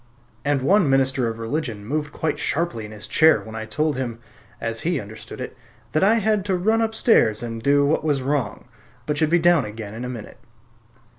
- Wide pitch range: Yes, wide, 6.0 semitones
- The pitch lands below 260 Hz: Yes, medium, 140 Hz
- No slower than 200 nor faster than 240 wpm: Yes, fast, 205 wpm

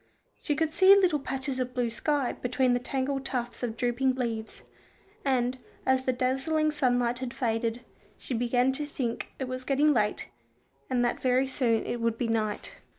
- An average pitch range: No, narrow, 2.0 semitones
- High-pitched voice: Yes, very high, 255 Hz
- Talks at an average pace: Yes, average, 175 wpm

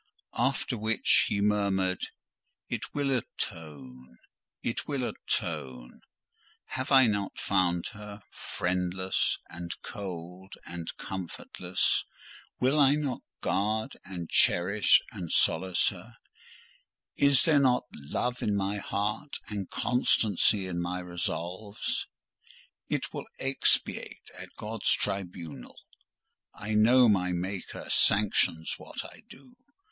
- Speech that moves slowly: Yes, slow, 110 wpm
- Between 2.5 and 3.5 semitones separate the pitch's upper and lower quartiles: No, average, 4.1 semitones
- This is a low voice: Yes, low, 100 Hz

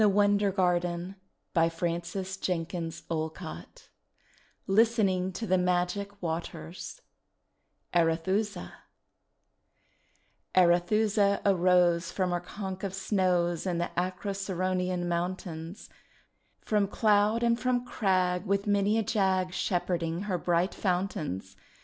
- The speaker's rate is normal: No, slow, 100 wpm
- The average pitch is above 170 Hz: Yes, medium, 185 Hz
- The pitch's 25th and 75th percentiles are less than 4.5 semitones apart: Yes, narrow, 2.5 semitones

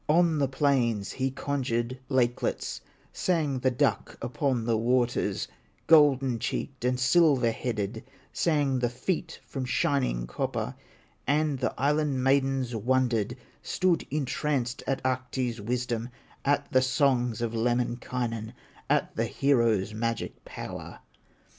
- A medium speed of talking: No, slow, 120 wpm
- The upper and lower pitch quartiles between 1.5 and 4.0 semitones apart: Yes, average, 2.8 semitones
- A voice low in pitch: Yes, low, 130 Hz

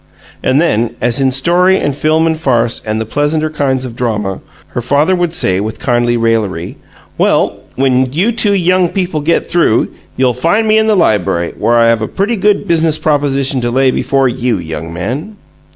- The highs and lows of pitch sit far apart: Yes, wide, 6.1 semitones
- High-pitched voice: No, low, 135 Hz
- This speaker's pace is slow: No, average, 190 wpm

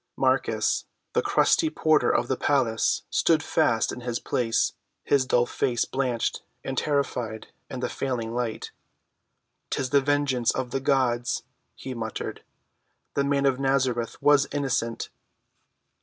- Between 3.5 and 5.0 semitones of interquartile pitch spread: No, average, 2.7 semitones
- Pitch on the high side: No, low, 130 Hz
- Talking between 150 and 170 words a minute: No, slow, 135 wpm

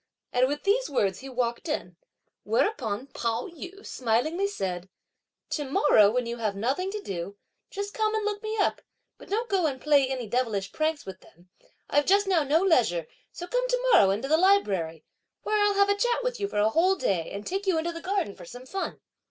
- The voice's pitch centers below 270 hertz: No, very high, 295 Hz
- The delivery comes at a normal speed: No, fast, 210 wpm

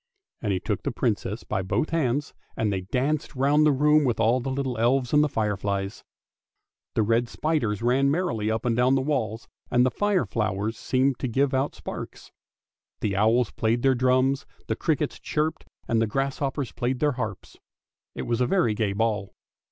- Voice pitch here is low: Yes, low, 125 Hz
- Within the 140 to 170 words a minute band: No, average, 190 wpm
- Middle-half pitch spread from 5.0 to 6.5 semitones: No, average, 3.7 semitones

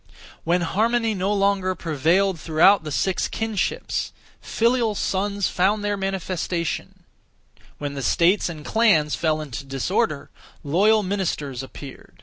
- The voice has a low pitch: No, medium, 185 Hz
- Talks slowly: Yes, slow, 125 wpm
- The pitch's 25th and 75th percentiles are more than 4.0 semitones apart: Yes, average, 4.6 semitones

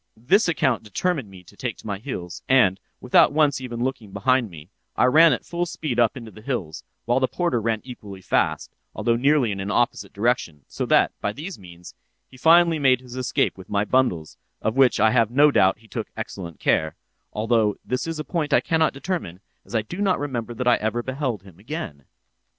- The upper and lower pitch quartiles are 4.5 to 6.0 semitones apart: Yes, wide, 5.5 semitones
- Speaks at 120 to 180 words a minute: No, fast, 205 wpm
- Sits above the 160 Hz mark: No, low, 120 Hz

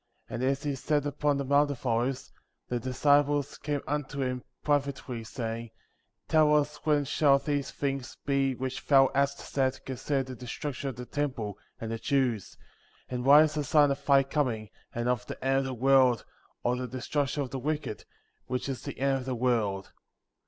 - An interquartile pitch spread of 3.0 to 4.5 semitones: No, narrow, 2.4 semitones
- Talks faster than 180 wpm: Yes, average, 190 wpm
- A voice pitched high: No, low, 135 Hz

